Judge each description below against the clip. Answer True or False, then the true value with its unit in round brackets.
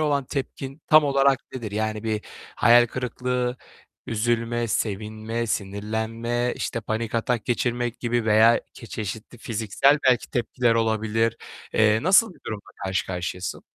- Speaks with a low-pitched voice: True (115 Hz)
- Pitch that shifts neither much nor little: False (2.2 semitones)